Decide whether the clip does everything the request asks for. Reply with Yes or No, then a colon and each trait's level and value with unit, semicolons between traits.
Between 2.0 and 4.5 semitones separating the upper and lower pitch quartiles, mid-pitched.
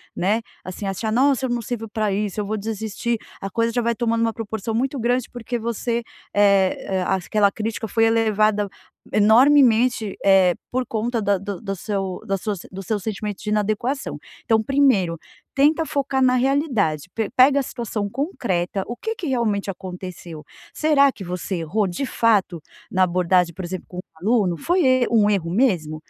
No: average, 3.9 semitones; high, 215 Hz